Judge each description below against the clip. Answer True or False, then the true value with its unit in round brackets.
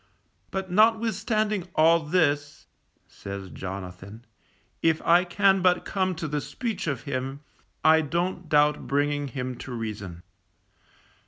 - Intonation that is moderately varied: False (6.3 semitones)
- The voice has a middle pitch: True (150 Hz)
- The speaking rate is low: True (120 wpm)